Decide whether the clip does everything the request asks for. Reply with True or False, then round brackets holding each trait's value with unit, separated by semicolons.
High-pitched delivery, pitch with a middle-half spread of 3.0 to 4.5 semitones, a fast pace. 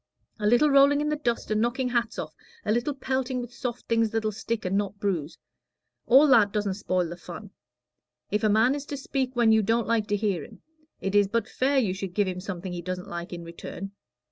True (220 Hz; 4.2 semitones; 225 wpm)